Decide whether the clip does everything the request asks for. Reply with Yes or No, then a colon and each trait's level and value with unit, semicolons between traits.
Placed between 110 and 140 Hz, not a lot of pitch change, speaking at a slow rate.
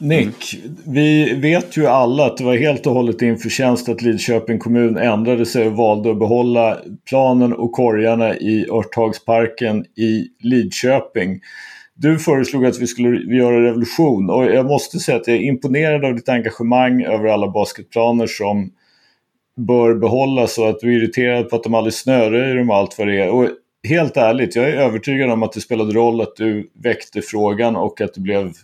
No: low, 115 Hz; narrow, 2.1 semitones; average, 180 wpm